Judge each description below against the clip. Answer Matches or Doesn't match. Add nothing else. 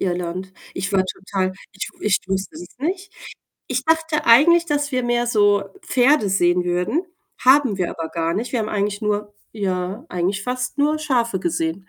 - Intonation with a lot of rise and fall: Matches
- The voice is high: Matches